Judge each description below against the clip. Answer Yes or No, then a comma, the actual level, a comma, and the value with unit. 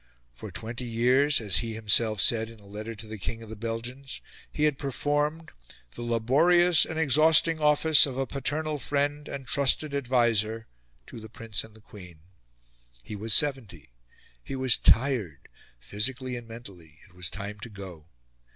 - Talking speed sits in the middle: Yes, average, 165 wpm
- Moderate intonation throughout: Yes, average, 4.7 semitones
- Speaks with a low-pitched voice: Yes, low, 120 Hz